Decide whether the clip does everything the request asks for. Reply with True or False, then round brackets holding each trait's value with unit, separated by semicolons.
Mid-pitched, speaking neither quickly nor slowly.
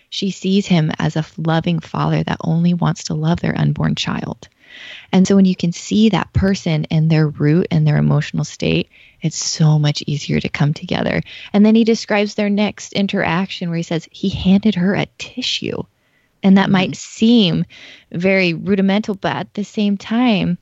True (180 Hz; 185 wpm)